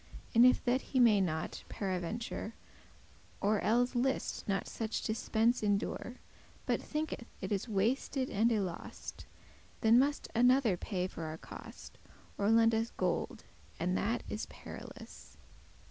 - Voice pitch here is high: Yes, high, 225 Hz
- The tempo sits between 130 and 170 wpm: Yes, average, 140 wpm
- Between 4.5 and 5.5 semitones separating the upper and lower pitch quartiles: No, average, 3.6 semitones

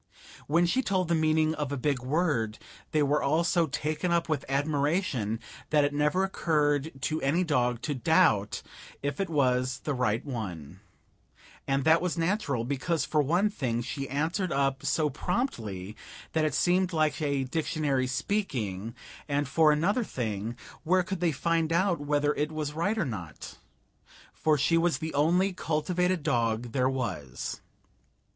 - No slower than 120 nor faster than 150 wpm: No, average, 160 wpm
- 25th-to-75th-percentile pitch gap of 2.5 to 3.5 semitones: No, average, 4.4 semitones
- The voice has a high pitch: No, medium, 150 Hz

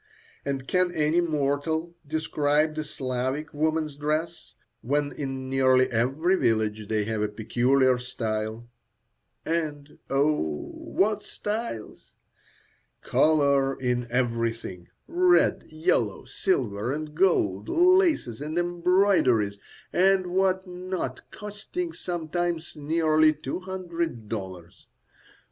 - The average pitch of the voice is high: No, medium, 150 Hz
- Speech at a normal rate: No, slow, 100 wpm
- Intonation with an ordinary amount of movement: No, wide, 6.1 semitones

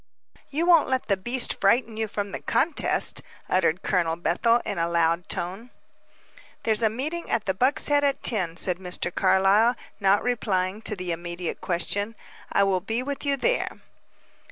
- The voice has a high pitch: Yes, high, 205 Hz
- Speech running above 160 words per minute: Yes, average, 170 wpm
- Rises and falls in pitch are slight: No, average, 5.2 semitones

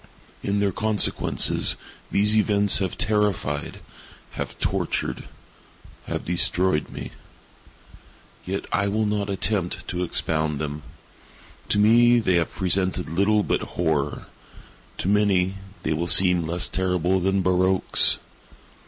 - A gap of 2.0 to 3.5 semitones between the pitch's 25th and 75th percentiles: Yes, average, 2.8 semitones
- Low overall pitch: Yes, very low, 95 Hz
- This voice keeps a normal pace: No, slow, 110 wpm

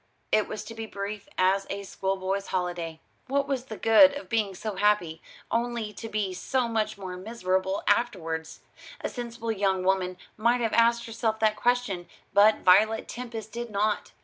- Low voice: No, high, 215 Hz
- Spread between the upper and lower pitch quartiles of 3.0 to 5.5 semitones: Yes, average, 3.4 semitones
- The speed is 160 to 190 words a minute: Yes, average, 170 wpm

